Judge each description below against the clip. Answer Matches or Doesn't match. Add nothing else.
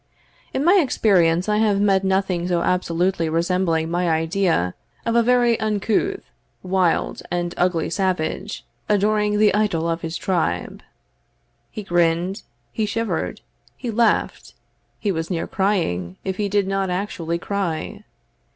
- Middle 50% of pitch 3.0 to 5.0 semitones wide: Matches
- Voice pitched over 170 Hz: Matches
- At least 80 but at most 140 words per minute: Matches